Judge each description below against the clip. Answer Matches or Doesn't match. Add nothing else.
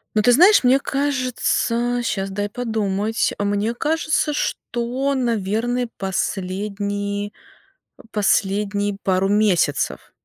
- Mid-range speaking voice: Doesn't match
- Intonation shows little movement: Doesn't match